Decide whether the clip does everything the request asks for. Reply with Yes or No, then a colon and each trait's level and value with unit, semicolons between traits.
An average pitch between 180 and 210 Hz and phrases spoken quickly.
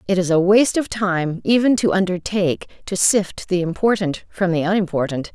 No: medium, 185 Hz; average, 180 wpm